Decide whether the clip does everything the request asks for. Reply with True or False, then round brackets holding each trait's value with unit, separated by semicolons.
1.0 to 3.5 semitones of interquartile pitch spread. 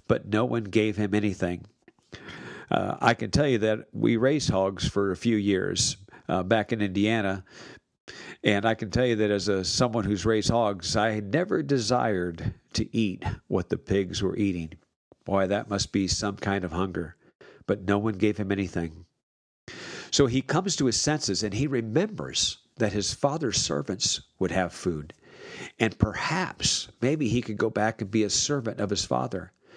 True (3.1 semitones)